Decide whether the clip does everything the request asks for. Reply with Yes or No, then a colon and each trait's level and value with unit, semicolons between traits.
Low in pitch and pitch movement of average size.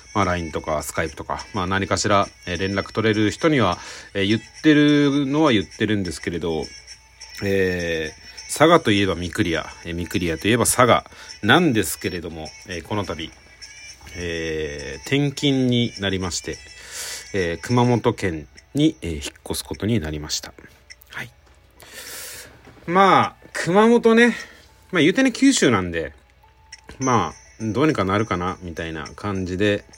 No: low, 100 Hz; wide, 5.8 semitones